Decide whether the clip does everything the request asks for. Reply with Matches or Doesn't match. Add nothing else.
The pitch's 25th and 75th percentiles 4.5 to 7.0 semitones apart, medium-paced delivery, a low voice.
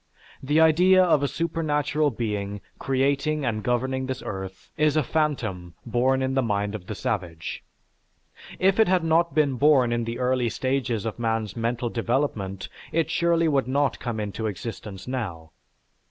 Matches